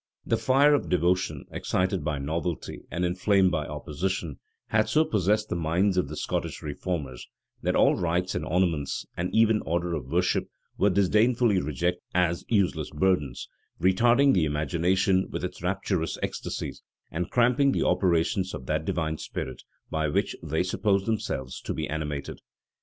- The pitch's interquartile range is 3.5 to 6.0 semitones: Yes, average, 3.9 semitones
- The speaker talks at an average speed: Yes, average, 155 wpm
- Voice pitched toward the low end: Yes, very low, 90 Hz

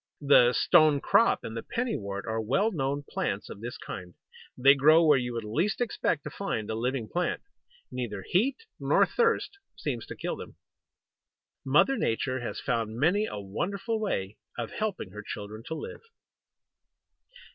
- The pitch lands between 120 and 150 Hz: Yes, low, 135 Hz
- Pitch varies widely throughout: Yes, wide, 8.3 semitones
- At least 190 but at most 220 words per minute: No, average, 165 wpm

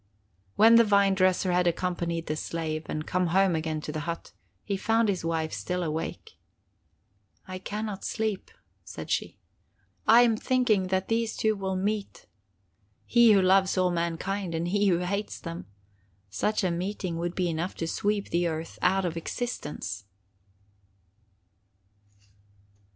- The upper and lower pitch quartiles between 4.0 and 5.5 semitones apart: No, average, 3.4 semitones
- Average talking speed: Yes, average, 150 wpm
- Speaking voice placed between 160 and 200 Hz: Yes, medium, 185 Hz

